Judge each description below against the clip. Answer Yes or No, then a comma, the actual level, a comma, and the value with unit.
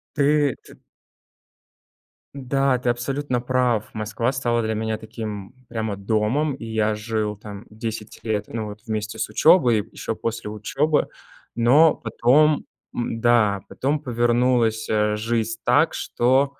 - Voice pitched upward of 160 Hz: No, low, 115 Hz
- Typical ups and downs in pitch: Yes, average, 3.0 semitones